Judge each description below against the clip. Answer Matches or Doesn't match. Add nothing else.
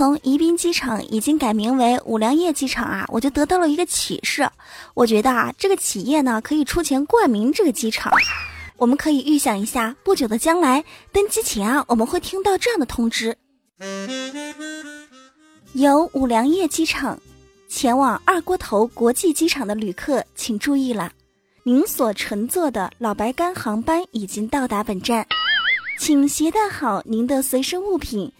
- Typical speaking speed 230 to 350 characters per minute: Matches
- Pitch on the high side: Matches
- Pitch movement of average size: Doesn't match